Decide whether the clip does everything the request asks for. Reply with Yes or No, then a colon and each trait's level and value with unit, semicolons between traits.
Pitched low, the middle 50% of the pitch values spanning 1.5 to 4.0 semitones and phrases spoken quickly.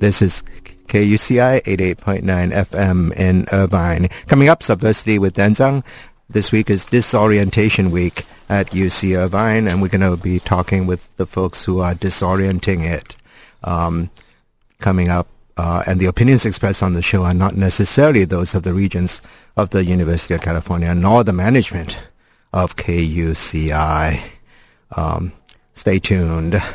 No: very low, 95 Hz; narrow, 2.6 semitones; average, 145 wpm